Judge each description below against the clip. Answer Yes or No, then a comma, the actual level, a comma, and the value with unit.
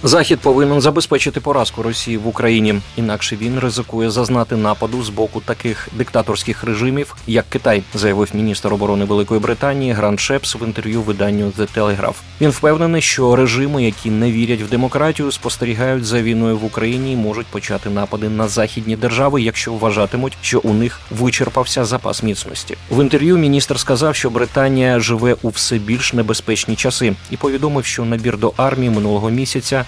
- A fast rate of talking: Yes, fast, 160 wpm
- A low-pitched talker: Yes, low, 115 Hz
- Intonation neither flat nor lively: Yes, average, 3.0 semitones